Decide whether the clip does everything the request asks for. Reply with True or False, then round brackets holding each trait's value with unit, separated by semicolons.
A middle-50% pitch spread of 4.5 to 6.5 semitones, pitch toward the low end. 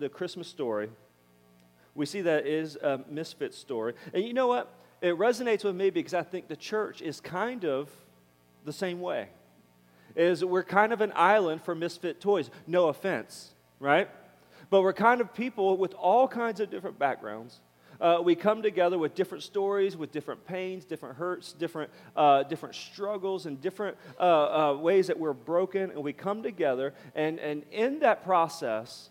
False (5.0 semitones; 175 Hz)